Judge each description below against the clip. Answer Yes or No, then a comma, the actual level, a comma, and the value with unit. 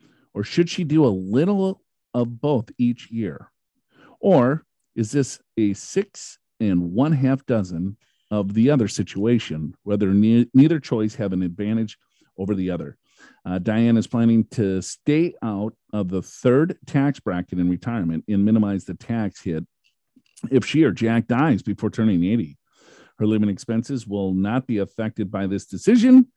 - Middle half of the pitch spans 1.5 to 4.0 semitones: No, average, 4.5 semitones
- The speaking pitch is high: No, low, 110 Hz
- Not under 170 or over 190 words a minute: No, average, 160 wpm